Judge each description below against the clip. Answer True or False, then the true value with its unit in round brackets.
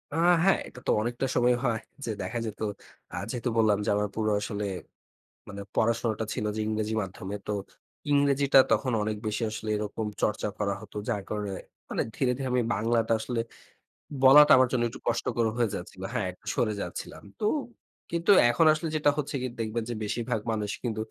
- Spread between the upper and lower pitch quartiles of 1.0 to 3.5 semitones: True (3.0 semitones)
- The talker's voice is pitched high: False (115 Hz)